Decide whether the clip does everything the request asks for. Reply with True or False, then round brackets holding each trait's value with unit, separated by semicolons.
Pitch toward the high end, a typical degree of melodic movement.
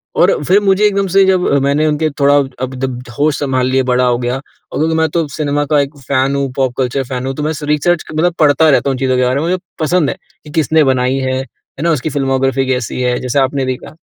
False (140 Hz; 3.1 semitones)